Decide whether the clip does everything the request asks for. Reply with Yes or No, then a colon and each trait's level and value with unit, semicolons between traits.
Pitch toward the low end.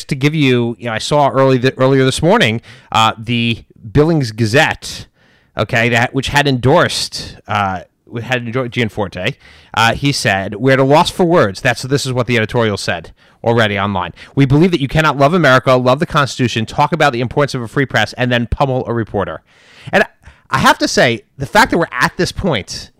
Yes: low, 130 Hz